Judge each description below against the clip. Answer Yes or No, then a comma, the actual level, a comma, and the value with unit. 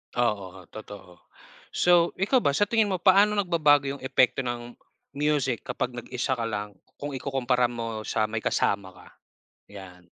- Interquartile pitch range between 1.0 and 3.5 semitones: No, wide, 5.5 semitones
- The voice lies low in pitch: Yes, low, 125 Hz